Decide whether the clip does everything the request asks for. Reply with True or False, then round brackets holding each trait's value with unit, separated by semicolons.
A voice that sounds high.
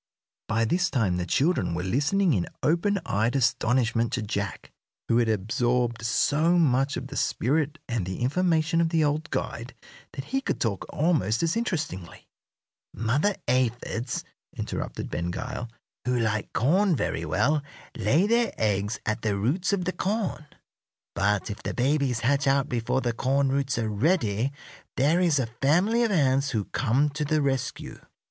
False (130 Hz)